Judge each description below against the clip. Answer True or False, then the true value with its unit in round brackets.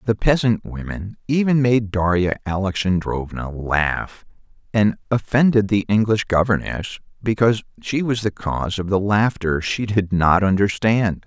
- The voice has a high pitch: False (100 Hz)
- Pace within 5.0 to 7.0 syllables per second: False (4.5 syllables/s)